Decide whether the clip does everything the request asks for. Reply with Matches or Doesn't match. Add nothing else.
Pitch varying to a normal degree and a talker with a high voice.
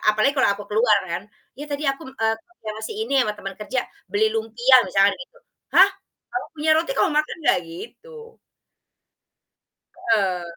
Doesn't match